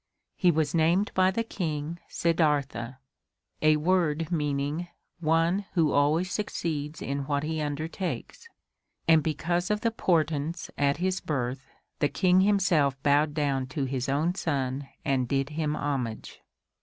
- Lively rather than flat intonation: No, average, 3.3 semitones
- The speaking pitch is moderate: Yes, medium, 155 Hz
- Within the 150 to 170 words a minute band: No, average, 140 wpm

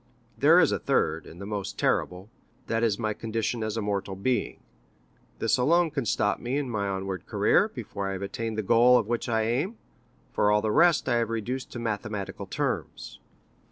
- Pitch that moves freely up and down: No, average, 3.1 semitones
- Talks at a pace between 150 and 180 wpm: No, average, 190 wpm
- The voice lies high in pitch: No, low, 110 Hz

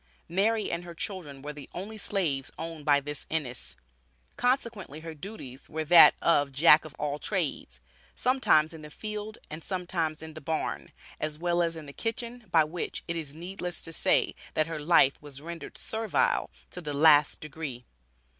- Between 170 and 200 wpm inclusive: Yes, average, 175 wpm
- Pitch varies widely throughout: No, average, 3.4 semitones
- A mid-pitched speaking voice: Yes, medium, 160 Hz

